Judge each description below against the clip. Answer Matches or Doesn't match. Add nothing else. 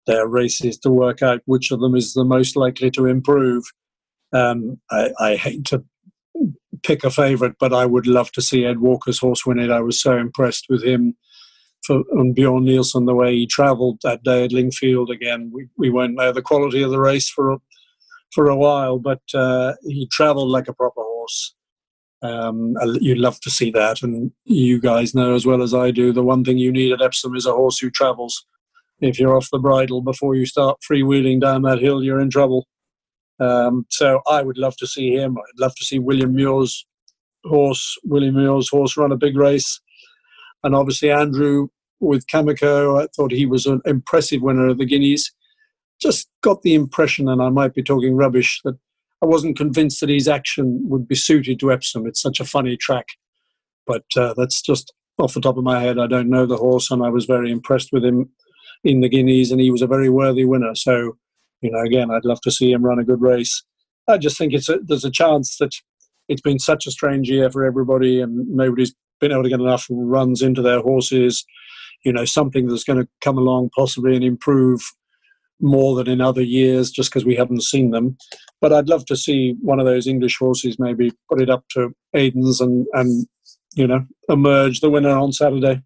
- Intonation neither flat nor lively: Doesn't match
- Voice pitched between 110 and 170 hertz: Matches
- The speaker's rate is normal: Doesn't match